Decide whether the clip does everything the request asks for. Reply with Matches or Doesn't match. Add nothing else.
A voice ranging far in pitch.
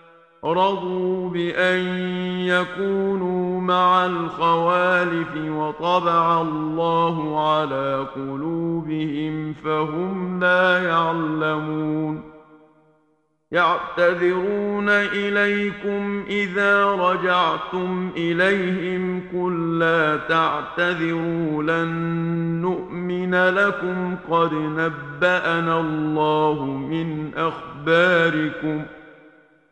Doesn't match